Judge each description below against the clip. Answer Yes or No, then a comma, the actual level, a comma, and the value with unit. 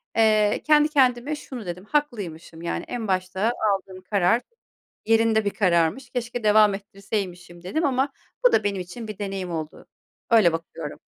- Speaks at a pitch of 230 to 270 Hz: No, high, 205 Hz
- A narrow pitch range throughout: No, average, 4.7 semitones